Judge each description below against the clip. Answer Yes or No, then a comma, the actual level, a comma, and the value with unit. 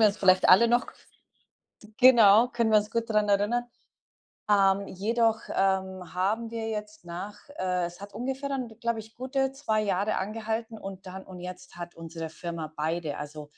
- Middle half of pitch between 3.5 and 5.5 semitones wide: Yes, average, 3.8 semitones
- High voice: Yes, high, 205 Hz